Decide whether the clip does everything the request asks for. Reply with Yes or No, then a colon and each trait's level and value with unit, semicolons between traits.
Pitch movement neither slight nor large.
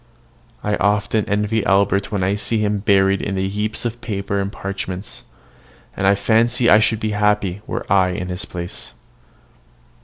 No: narrow, 1.4 semitones